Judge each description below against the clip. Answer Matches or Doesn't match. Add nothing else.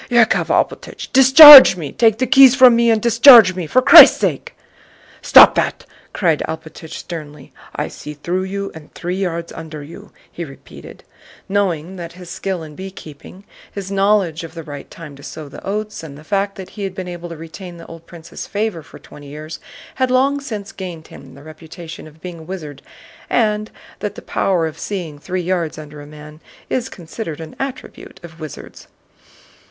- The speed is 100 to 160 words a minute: Doesn't match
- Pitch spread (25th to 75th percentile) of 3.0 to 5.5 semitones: Matches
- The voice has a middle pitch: Matches